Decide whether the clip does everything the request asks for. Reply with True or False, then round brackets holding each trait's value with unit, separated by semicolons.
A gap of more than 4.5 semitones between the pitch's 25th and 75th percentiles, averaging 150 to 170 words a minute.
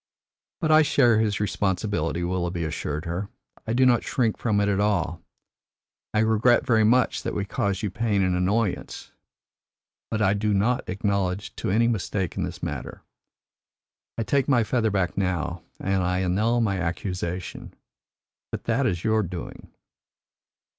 False (3.6 semitones; 155 wpm)